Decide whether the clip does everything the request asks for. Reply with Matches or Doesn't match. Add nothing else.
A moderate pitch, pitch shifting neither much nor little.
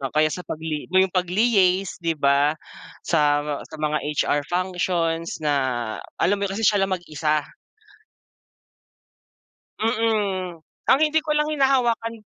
Doesn't match